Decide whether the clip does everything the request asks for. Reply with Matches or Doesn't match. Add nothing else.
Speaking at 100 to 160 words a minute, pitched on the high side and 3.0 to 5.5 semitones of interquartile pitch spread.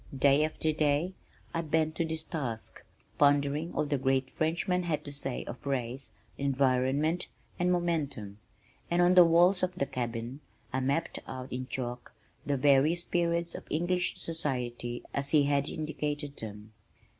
Doesn't match